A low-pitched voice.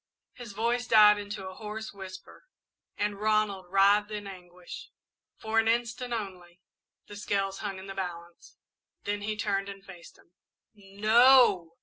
No: high, 205 Hz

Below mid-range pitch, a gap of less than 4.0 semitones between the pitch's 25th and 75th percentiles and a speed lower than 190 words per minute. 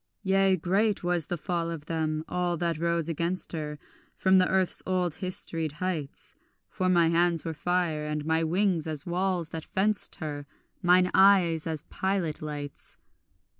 No: medium, 170 Hz; average, 2.7 semitones; average, 160 wpm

